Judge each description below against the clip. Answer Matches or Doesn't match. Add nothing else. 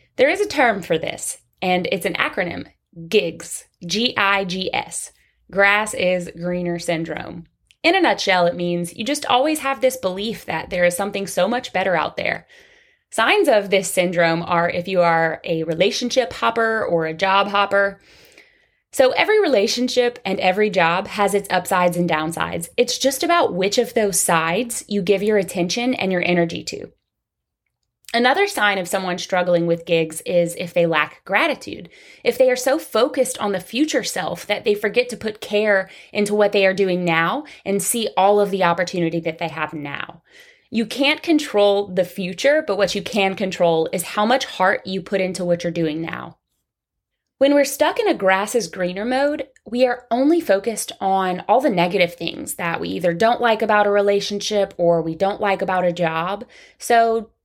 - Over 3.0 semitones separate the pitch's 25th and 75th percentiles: Matches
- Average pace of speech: Matches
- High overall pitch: Matches